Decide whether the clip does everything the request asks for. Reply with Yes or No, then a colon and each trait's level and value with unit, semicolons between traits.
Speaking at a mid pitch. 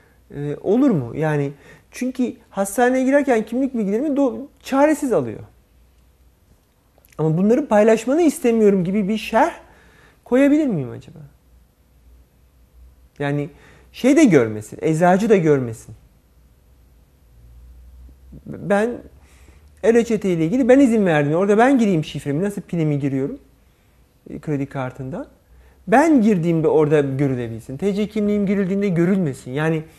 Yes: medium, 160 Hz